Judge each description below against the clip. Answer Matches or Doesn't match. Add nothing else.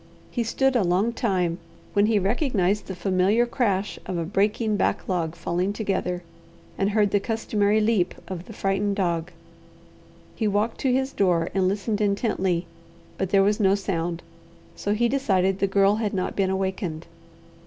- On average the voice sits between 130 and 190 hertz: Doesn't match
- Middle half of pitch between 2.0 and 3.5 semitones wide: Matches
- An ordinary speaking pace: Matches